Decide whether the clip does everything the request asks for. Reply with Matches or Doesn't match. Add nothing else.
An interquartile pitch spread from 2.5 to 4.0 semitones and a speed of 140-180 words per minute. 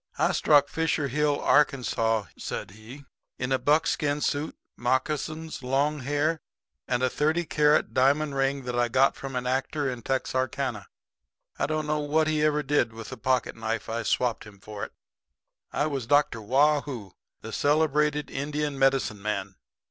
Matches